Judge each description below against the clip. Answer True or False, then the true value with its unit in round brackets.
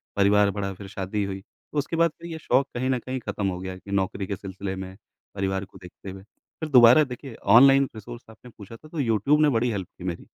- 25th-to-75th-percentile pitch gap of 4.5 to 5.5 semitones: True (5.1 semitones)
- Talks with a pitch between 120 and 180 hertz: False (105 Hz)